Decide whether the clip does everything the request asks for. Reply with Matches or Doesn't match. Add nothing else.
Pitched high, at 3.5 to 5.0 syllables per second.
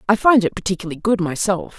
Doesn't match